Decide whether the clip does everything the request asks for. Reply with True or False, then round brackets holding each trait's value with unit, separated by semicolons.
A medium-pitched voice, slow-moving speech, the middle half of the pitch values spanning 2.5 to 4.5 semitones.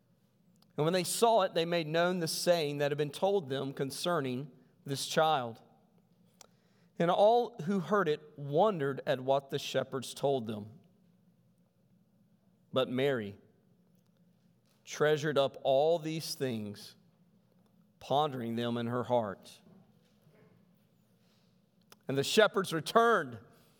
False (170 Hz; 115 wpm; 5.1 semitones)